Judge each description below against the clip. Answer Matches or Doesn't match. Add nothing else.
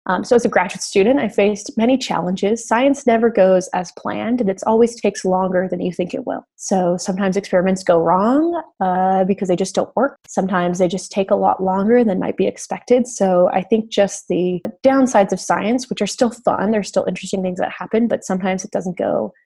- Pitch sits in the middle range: Doesn't match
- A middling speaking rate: Doesn't match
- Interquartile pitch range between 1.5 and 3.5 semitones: Doesn't match